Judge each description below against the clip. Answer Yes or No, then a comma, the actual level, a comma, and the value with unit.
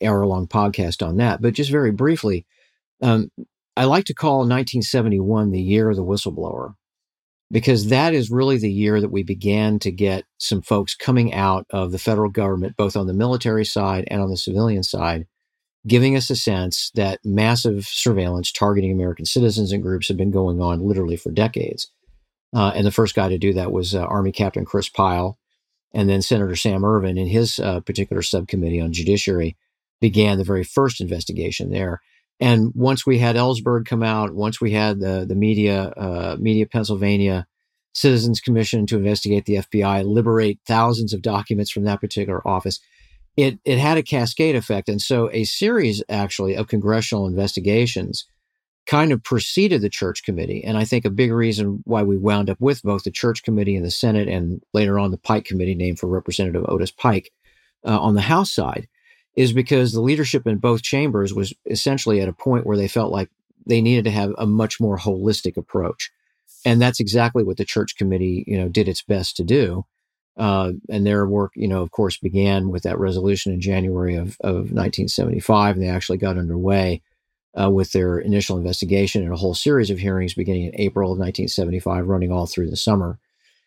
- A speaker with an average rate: Yes, average, 190 wpm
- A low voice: Yes, low, 105 Hz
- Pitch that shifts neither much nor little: Yes, average, 3.2 semitones